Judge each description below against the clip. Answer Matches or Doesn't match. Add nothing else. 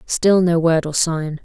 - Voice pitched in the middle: Matches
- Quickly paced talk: Matches